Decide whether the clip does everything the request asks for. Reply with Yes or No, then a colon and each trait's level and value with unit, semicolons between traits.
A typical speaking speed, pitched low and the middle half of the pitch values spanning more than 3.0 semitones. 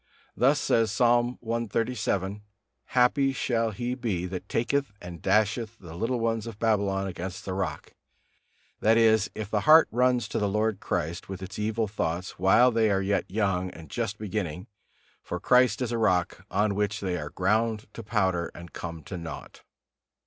Yes: average, 170 wpm; low, 105 Hz; average, 3.5 semitones